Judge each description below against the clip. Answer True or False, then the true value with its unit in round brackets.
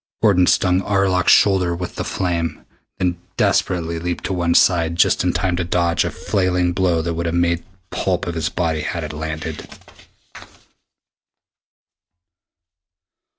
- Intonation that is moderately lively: False (1.5 semitones)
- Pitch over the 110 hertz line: False (85 Hz)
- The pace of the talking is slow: False (145 wpm)